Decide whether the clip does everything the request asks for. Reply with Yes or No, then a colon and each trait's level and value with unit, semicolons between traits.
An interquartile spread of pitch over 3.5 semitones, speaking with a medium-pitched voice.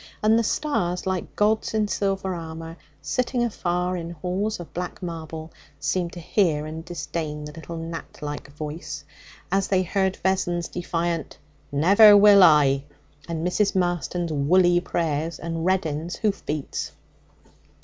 No: average, 2.9 semitones; medium, 175 Hz